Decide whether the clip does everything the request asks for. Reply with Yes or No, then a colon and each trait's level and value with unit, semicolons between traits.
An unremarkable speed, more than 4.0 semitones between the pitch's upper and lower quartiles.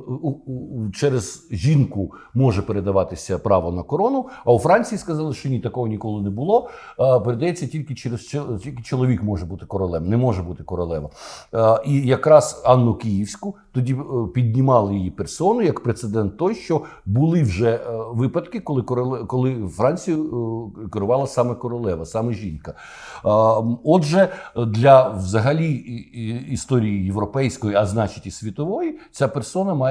Yes: average, 130 wpm; average, 4.6 semitones